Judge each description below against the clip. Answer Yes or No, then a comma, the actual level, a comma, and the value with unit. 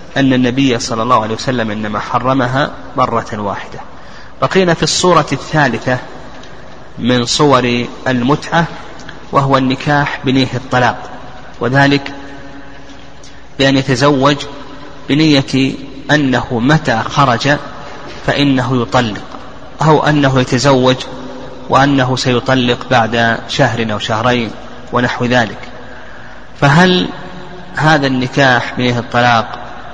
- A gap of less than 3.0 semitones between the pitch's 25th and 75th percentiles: Yes, narrow, 2.5 semitones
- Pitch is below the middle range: Yes, low, 130 Hz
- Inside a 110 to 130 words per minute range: No, average, 90 wpm